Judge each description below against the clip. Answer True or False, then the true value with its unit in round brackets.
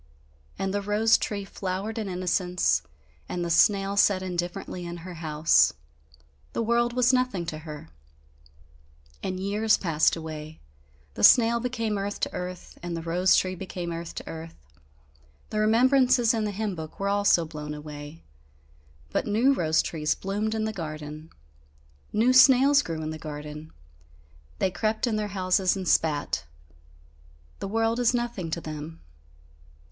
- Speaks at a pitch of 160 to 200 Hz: True (185 Hz)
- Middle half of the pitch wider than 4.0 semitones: True (5.0 semitones)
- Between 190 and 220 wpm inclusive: False (150 wpm)